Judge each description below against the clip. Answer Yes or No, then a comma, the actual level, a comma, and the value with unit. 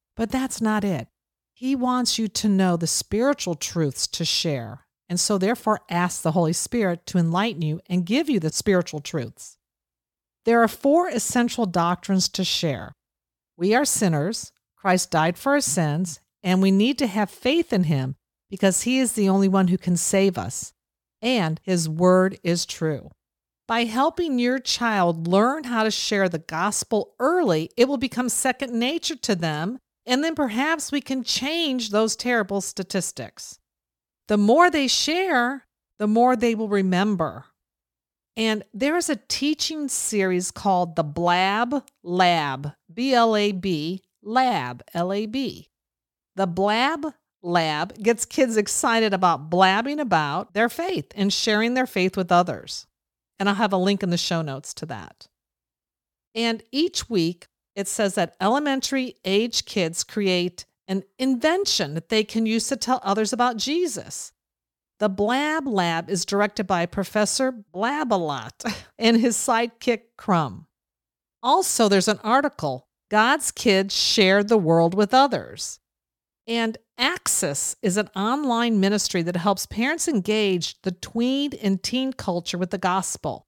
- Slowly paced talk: No, average, 150 wpm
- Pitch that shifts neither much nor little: No, wide, 5.8 semitones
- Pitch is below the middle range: No, high, 200 Hz